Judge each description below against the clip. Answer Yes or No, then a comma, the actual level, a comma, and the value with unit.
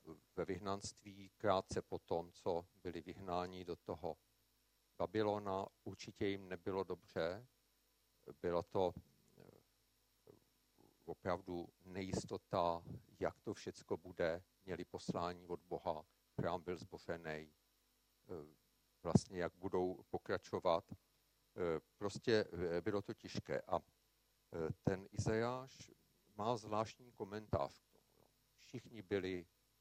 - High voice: No, very low, 95 Hz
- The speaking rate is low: Yes, slow, 95 wpm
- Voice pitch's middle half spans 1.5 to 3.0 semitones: No, average, 3.5 semitones